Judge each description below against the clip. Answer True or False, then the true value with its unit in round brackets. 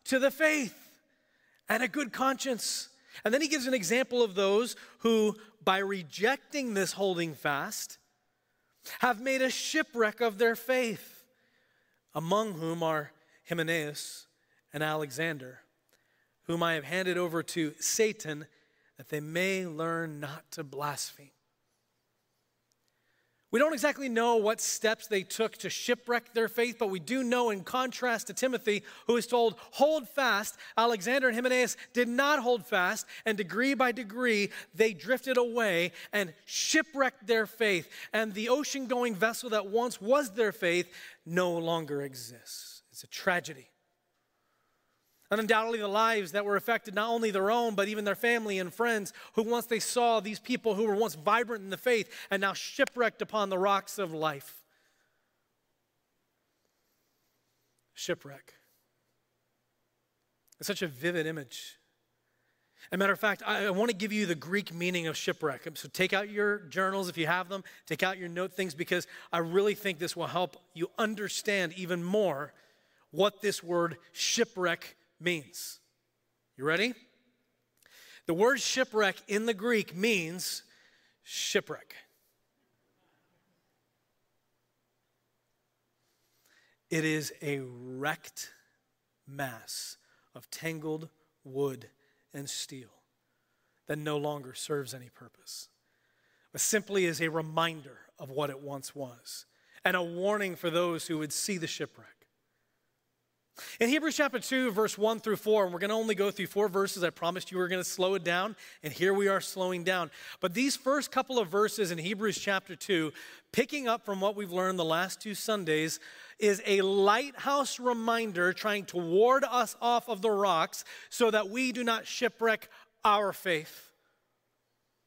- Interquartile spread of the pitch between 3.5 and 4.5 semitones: False (5.5 semitones)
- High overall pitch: True (200 Hz)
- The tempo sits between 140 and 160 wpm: True (150 wpm)